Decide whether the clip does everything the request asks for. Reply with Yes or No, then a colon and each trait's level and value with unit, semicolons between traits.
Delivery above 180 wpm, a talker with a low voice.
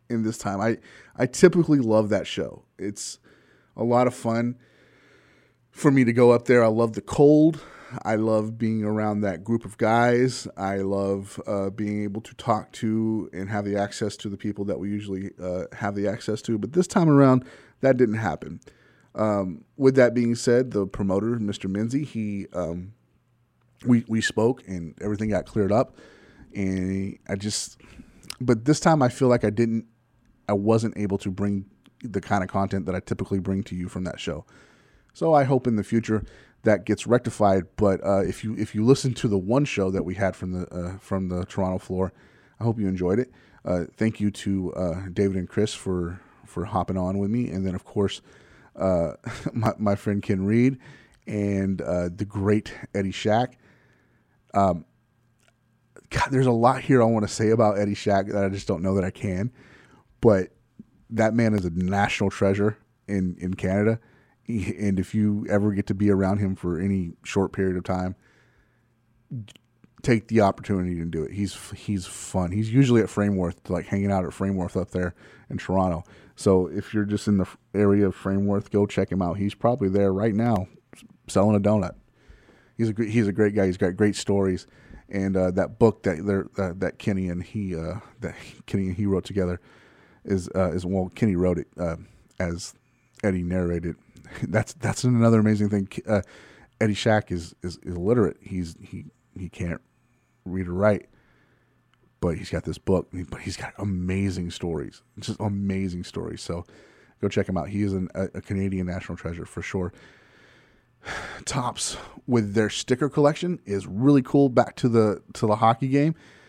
Yes: average, 190 wpm; low, 100 Hz